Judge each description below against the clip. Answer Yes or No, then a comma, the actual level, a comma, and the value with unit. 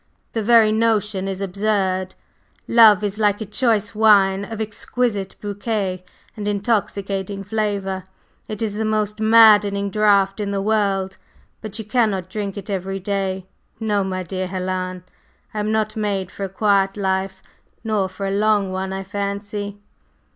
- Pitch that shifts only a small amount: Yes, narrow, 1.8 semitones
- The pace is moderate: Yes, average, 155 wpm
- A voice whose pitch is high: Yes, high, 200 Hz